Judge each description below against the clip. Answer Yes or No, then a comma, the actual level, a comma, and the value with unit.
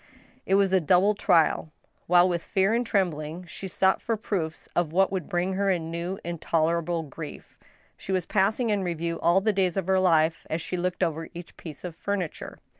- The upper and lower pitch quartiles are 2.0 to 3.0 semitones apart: Yes, narrow, 2.5 semitones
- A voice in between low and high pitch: Yes, medium, 180 Hz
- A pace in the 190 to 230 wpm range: Yes, average, 195 wpm